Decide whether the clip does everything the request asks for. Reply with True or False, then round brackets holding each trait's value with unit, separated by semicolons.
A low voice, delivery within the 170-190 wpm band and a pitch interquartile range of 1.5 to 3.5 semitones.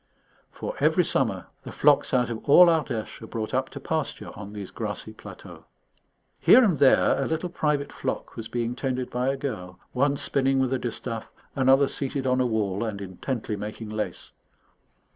False (125 Hz; 180 wpm; 4.0 semitones)